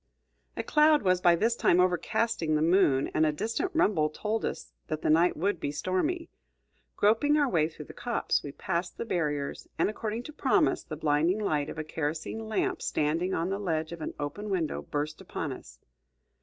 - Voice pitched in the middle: Yes, medium, 175 Hz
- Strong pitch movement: Yes, wide, 5.8 semitones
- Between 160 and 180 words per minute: No, average, 195 wpm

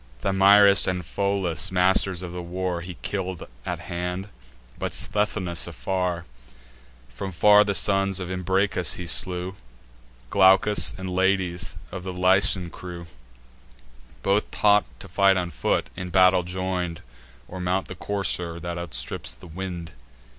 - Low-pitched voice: Yes, very low, 90 Hz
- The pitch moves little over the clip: Yes, narrow, 1.6 semitones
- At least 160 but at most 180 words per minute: No, slow, 135 wpm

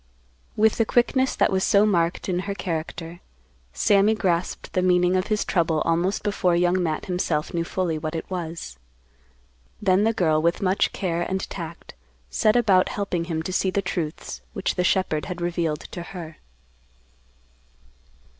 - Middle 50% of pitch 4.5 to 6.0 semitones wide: No, average, 2.7 semitones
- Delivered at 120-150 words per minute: No, average, 165 wpm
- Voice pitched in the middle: Yes, medium, 180 Hz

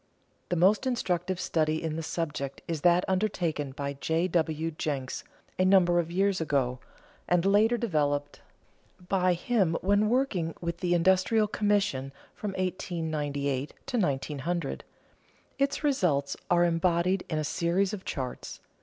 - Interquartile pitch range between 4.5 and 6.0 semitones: No, average, 3.8 semitones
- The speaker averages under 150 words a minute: Yes, average, 140 wpm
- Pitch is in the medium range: Yes, medium, 175 Hz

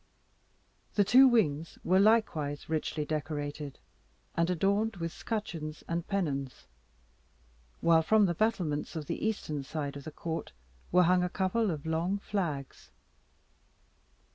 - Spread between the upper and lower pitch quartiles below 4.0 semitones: No, average, 4.7 semitones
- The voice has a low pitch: No, medium, 165 Hz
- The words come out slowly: Yes, slow, 130 wpm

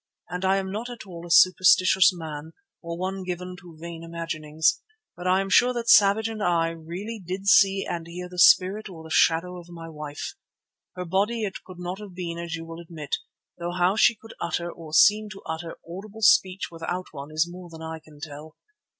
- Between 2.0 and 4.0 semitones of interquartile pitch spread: Yes, average, 2.7 semitones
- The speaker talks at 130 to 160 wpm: No, fast, 205 wpm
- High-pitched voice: No, medium, 175 Hz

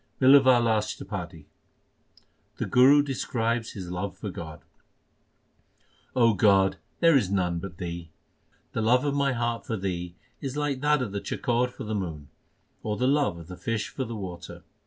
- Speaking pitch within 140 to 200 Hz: No, low, 110 Hz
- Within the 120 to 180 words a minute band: Yes, average, 160 wpm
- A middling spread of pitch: No, wide, 5.9 semitones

